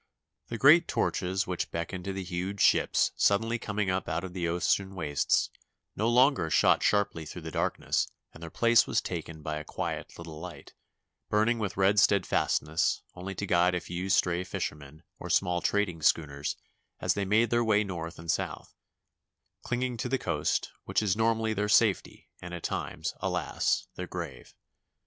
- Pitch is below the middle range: Yes, very low, 95 Hz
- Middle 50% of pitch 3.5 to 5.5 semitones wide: Yes, average, 4.0 semitones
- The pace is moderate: Yes, average, 170 wpm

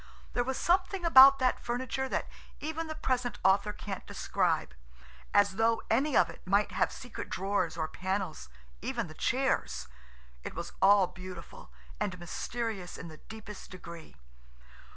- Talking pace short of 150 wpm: Yes, average, 140 wpm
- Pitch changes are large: Yes, wide, 6.3 semitones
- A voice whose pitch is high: Yes, high, 205 Hz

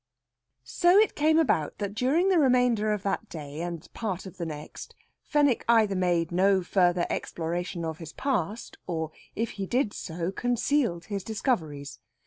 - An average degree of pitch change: No, wide, 6.3 semitones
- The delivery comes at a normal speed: Yes, average, 160 wpm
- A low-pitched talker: No, high, 195 Hz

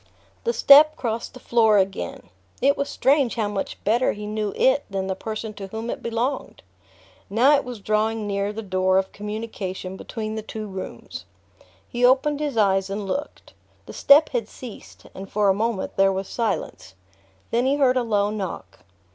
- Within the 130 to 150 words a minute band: No, average, 180 wpm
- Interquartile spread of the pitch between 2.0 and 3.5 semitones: No, average, 4.0 semitones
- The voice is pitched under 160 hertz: No, high, 220 Hz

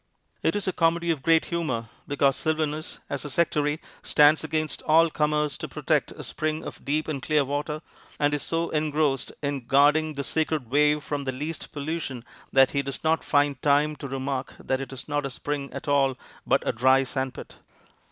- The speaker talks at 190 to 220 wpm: Yes, average, 195 wpm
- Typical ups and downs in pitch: No, narrow, 2.2 semitones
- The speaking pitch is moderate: Yes, medium, 145 Hz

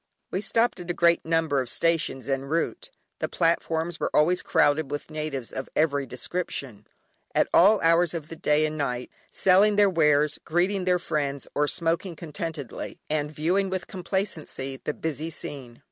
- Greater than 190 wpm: No, average, 165 wpm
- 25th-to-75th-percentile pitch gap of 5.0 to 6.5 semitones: No, average, 3.3 semitones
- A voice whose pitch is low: No, medium, 160 Hz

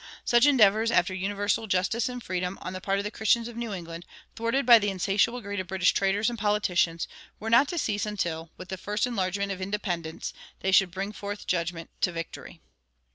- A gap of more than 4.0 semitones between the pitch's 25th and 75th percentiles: No, average, 3.3 semitones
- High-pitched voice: Yes, high, 200 Hz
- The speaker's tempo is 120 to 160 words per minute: No, average, 200 wpm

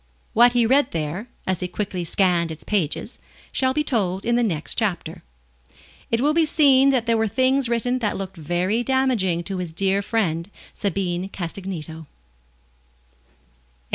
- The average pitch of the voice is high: Yes, high, 200 Hz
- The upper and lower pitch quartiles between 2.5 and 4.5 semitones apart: No, wide, 5.6 semitones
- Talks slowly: No, average, 155 wpm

